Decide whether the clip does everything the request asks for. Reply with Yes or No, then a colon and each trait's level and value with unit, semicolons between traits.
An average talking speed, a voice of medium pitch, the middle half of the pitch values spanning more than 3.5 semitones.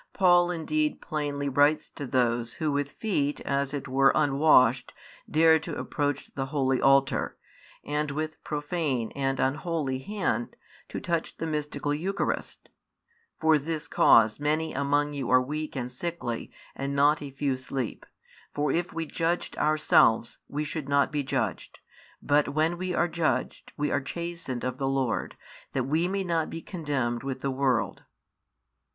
No: average, 155 wpm; medium, 145 Hz; average, 2.9 semitones